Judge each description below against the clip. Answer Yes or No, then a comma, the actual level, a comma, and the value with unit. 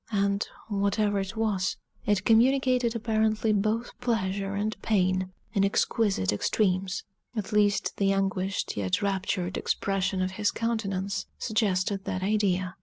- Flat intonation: Yes, narrow, 2.3 semitones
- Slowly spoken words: Yes, slow, 125 wpm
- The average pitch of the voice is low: No, high, 200 Hz